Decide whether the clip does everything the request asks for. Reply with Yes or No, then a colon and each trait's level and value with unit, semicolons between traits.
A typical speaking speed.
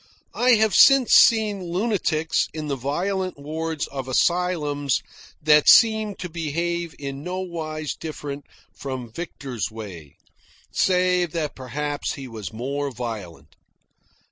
No: slow, 120 wpm